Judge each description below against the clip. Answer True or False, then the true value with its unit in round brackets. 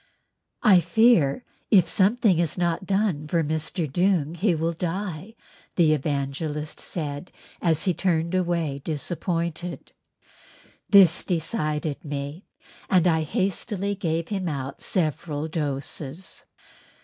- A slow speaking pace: True (115 wpm)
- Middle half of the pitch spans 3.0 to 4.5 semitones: True (3.5 semitones)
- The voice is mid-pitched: True (165 Hz)